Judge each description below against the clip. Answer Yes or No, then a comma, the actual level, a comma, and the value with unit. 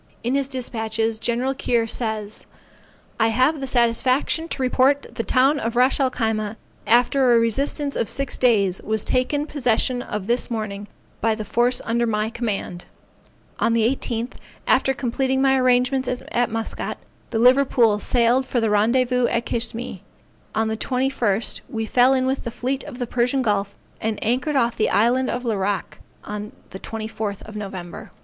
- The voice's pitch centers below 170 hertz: No, high, 235 Hz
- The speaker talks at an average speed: Yes, average, 165 wpm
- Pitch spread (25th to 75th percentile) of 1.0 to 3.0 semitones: Yes, average, 2.7 semitones